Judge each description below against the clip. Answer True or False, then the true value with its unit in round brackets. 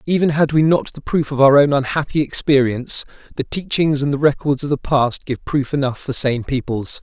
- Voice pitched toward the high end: False (140 Hz)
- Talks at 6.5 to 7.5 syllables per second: False (5.3 syllables/s)